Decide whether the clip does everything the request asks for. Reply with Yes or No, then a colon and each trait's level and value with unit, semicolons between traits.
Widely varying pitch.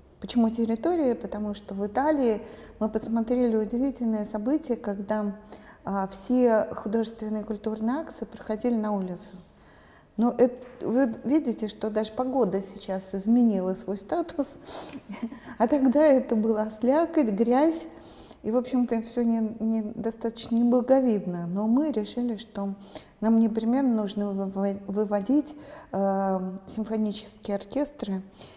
No: average, 3.2 semitones